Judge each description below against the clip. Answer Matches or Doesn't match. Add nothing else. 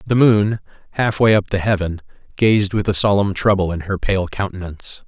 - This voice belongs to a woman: Doesn't match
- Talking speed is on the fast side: Doesn't match